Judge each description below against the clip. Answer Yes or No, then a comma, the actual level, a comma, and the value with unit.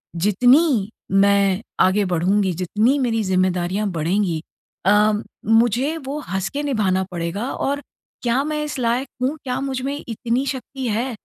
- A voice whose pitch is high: Yes, high, 220 Hz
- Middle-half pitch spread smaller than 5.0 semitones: No, wide, 5.5 semitones